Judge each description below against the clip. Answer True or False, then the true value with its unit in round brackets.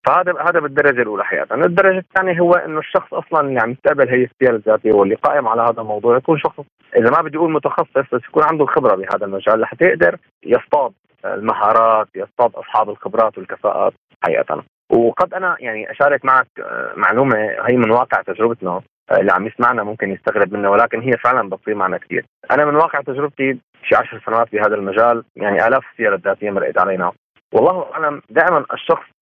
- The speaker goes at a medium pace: False (175 wpm)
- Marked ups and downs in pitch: True (6.0 semitones)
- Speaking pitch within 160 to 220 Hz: False (140 Hz)